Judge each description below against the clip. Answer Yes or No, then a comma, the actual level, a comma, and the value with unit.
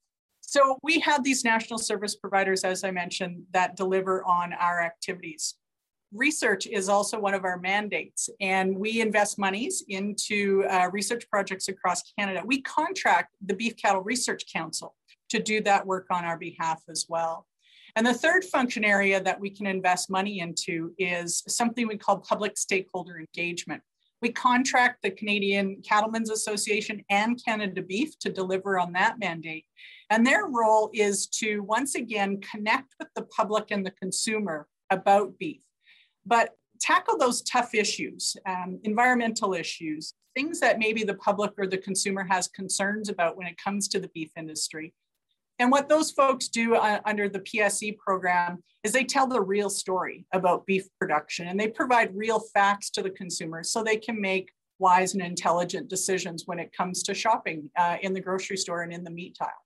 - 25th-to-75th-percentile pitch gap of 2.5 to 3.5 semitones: Yes, average, 3.1 semitones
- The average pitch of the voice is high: Yes, high, 200 Hz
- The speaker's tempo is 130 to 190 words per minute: Yes, average, 175 wpm